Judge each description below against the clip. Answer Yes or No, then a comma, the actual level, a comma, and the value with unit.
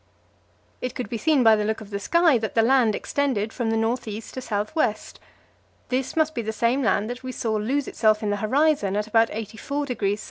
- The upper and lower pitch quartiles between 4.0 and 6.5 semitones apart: No, average, 3.5 semitones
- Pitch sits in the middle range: No, high, 225 Hz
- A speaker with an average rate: No, fast, 215 wpm